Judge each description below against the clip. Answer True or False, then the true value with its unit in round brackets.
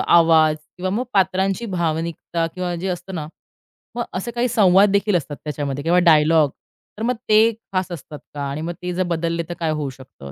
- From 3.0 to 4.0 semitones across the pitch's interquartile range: True (3.4 semitones)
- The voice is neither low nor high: True (170 Hz)